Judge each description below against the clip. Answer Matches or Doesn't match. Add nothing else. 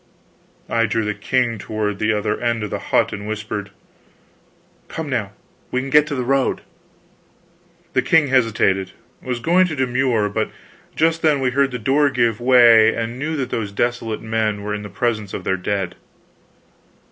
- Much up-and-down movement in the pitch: Doesn't match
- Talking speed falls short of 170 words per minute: Doesn't match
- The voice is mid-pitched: Doesn't match